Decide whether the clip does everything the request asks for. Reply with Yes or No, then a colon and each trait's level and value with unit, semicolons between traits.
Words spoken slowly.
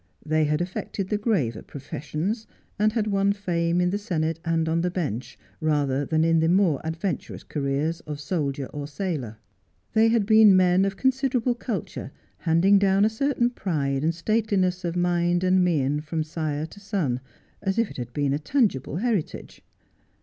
No: average, 170 wpm